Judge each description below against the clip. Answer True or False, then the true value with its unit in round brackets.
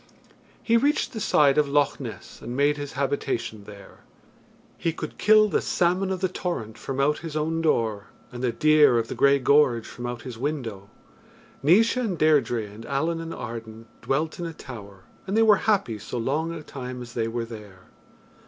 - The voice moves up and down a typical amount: False (6.0 semitones)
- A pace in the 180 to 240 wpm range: True (190 wpm)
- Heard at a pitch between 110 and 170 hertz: True (140 Hz)